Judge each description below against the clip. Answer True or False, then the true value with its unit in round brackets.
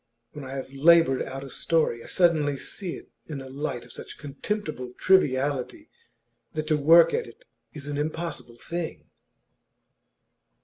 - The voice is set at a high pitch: False (145 Hz)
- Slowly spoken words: False (150 wpm)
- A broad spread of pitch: False (3.9 semitones)